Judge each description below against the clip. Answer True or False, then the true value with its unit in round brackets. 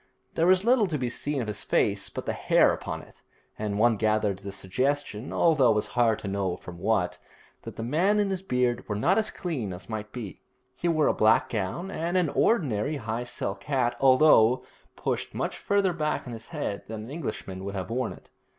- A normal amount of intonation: False (6.7 semitones)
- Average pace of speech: False (215 wpm)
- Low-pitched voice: True (120 Hz)